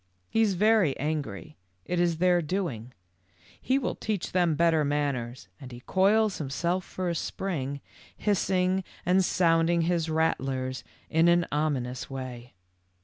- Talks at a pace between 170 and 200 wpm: No, average, 140 wpm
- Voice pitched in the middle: Yes, medium, 165 Hz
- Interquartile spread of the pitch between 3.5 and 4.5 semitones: No, average, 5.2 semitones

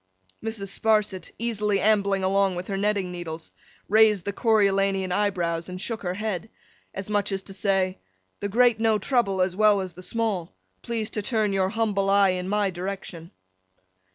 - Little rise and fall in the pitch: Yes, narrow, 2.2 semitones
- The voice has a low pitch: No, high, 200 Hz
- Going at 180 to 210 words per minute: No, average, 170 wpm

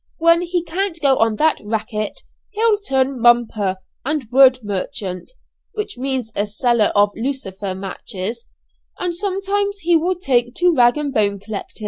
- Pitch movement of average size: No, wide, 8.0 semitones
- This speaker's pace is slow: No, average, 150 wpm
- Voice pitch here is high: Yes, very high, 260 Hz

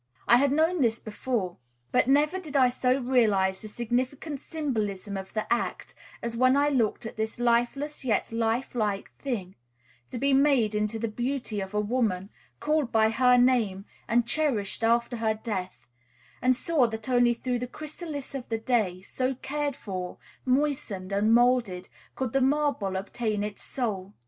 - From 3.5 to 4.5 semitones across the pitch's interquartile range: Yes, average, 3.9 semitones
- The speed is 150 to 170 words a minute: Yes, average, 165 wpm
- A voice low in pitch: No, high, 240 Hz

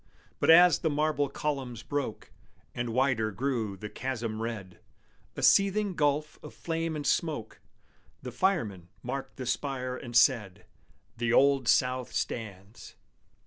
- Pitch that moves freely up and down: No, average, 4.5 semitones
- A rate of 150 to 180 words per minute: No, slow, 135 wpm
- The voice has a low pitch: Yes, low, 130 Hz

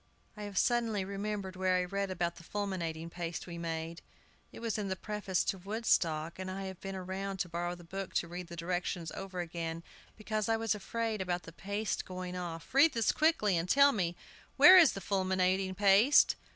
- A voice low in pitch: No, high, 190 Hz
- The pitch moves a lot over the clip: No, average, 2.9 semitones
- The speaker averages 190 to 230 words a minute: Yes, average, 200 wpm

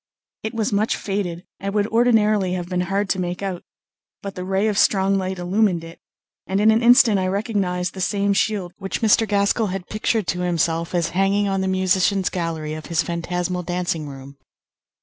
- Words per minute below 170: No, average, 190 wpm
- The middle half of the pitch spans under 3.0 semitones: Yes, narrow, 2.5 semitones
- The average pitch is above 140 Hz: Yes, high, 190 Hz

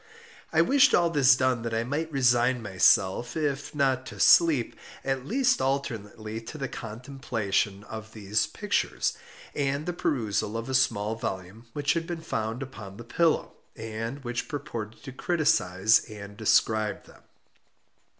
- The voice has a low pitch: Yes, low, 120 Hz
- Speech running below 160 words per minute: Yes, average, 150 wpm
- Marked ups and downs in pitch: No, average, 4.5 semitones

